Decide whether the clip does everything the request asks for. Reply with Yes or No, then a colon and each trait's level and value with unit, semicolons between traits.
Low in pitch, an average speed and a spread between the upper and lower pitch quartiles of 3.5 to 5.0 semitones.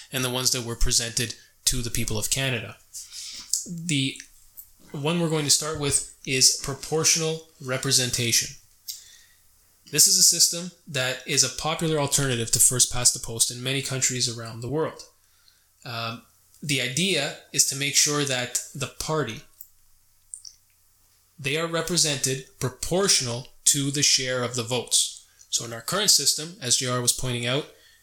Yes: low, 130 Hz; average, 145 wpm; average, 4.2 semitones